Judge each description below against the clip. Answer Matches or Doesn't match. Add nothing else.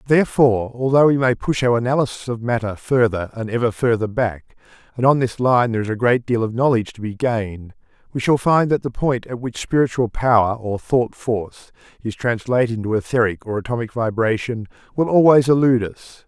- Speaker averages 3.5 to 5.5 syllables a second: Doesn't match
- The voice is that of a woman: Doesn't match